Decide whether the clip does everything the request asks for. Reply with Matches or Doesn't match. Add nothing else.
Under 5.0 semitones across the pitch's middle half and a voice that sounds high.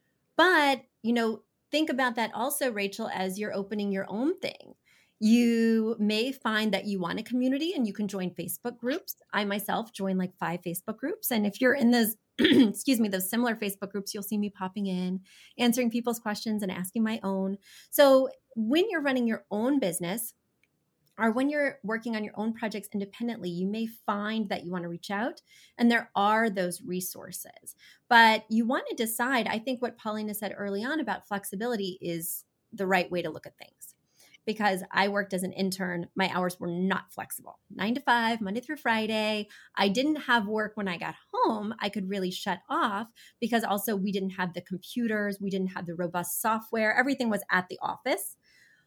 Matches